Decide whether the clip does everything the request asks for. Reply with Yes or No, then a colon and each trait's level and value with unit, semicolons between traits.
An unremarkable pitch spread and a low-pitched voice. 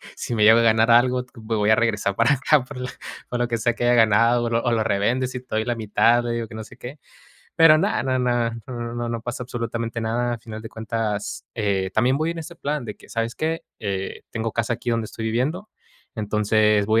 No: narrow, 2.0 semitones; low, 115 Hz